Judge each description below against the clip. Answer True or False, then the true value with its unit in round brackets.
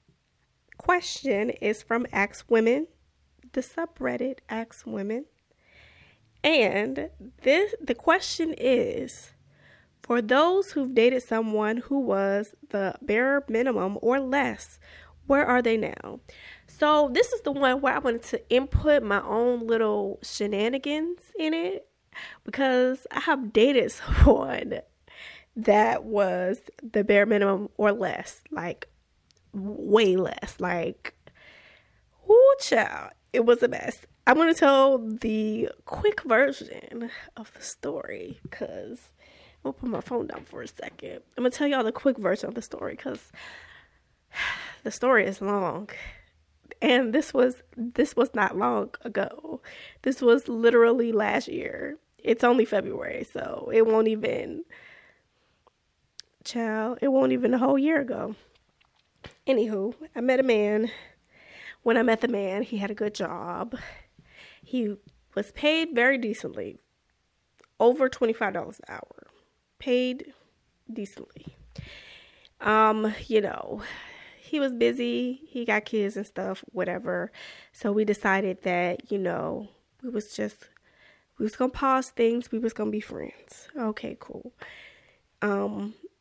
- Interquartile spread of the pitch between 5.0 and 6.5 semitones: False (4.2 semitones)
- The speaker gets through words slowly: True (130 wpm)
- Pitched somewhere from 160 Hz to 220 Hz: False (235 Hz)